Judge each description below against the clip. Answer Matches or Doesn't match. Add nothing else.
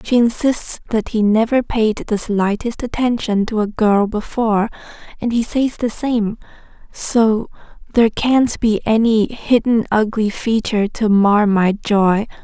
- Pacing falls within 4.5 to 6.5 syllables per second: Doesn't match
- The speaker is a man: Doesn't match